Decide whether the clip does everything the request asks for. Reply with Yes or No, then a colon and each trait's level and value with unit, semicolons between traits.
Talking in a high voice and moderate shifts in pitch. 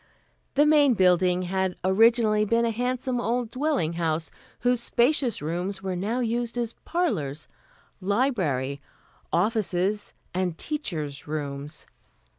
No: high, 205 Hz; wide, 5.7 semitones